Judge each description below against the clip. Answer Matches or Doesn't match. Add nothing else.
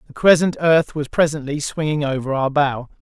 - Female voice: Doesn't match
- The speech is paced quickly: Doesn't match